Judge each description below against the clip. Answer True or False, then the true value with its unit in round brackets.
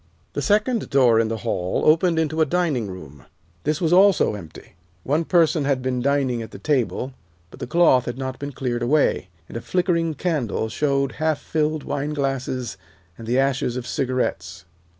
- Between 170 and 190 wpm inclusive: True (175 wpm)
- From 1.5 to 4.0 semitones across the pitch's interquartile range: False (4.7 semitones)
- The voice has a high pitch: False (135 Hz)